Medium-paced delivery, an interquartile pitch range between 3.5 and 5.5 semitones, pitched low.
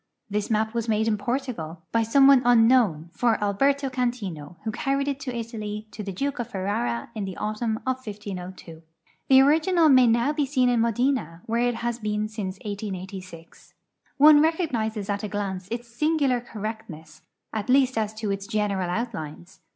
No: average, 175 wpm; average, 4.1 semitones; high, 220 Hz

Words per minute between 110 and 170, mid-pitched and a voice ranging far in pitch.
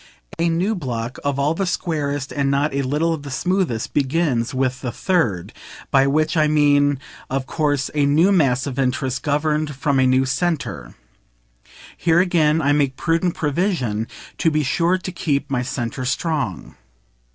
No: average, 165 wpm; medium, 145 Hz; average, 3.7 semitones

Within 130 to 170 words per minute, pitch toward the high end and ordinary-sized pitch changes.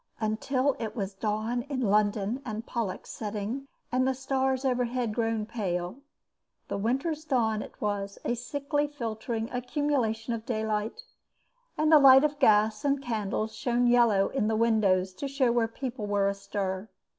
Yes: average, 155 wpm; high, 230 Hz; average, 3.7 semitones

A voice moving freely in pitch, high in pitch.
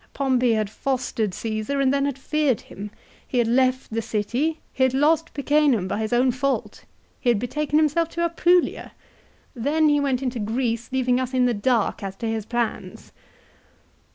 No: average, 3.7 semitones; very high, 255 Hz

